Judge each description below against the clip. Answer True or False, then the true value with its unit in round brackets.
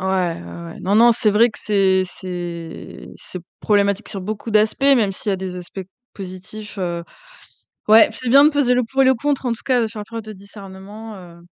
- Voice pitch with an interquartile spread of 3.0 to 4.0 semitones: True (3.5 semitones)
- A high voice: True (205 Hz)